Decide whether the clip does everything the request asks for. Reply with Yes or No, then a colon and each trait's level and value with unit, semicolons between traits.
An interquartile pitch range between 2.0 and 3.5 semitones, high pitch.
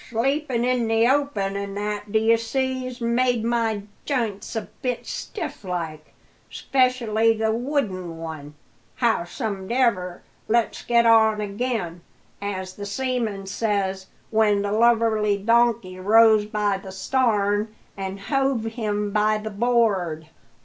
Yes: average, 3.0 semitones; high, 220 Hz